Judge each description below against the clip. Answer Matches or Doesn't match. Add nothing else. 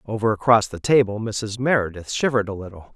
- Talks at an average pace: Matches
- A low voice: Matches